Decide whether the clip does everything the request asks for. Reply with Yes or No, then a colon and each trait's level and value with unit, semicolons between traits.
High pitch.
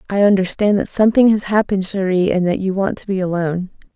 Yes: high, 195 Hz